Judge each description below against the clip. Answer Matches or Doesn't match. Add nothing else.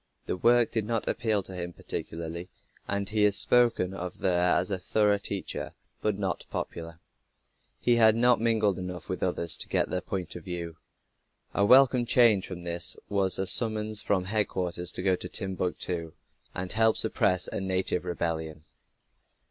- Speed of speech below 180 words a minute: Matches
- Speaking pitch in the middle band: Doesn't match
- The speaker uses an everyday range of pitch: Matches